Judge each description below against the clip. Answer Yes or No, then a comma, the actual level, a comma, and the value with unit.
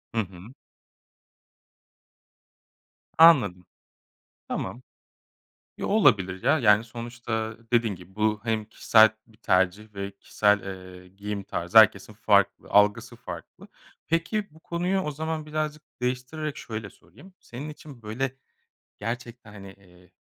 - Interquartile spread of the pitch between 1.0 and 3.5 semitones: No, average, 5.1 semitones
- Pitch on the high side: No, low, 110 Hz